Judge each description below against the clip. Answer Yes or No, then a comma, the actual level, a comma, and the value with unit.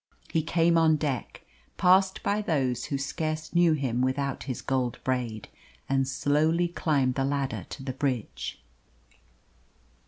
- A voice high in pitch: No, medium, 140 Hz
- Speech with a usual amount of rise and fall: Yes, average, 3.8 semitones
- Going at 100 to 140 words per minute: Yes, slow, 135 wpm